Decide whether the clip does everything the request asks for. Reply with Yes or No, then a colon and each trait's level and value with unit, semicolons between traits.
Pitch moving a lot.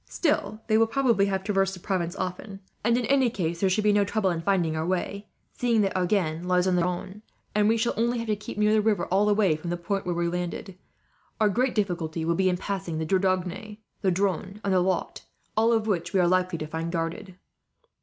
No: average, 3.1 semitones